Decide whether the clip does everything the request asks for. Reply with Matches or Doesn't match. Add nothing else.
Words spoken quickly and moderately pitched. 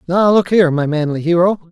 Matches